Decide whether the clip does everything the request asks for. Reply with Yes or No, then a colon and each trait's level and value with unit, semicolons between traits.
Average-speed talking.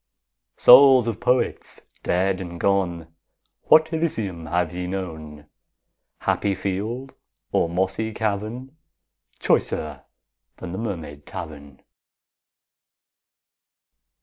No: slow, 90 wpm